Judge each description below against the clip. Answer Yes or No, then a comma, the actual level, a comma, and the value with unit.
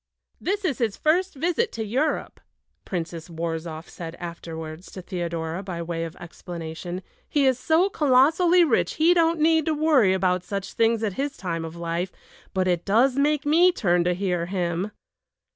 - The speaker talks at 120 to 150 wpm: No, average, 170 wpm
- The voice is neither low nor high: No, high, 195 Hz